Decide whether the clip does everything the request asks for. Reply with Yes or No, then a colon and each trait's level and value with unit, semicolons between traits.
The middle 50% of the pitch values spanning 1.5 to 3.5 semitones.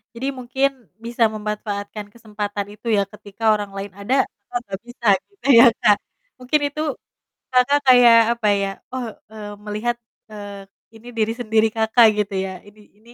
Yes: average, 2.8 semitones